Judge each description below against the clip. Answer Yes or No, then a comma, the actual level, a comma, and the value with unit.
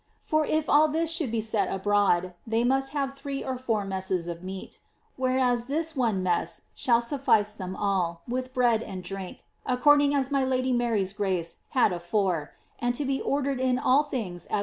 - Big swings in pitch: Yes, wide, 5.8 semitones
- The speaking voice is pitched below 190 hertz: No, high, 240 Hz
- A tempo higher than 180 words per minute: Yes, average, 200 wpm